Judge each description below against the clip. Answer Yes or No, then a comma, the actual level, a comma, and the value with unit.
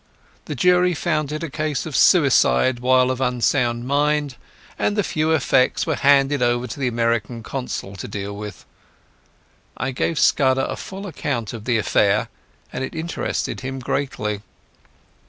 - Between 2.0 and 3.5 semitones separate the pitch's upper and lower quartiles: No, average, 4.0 semitones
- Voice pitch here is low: Yes, low, 130 Hz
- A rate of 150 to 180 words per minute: Yes, average, 155 wpm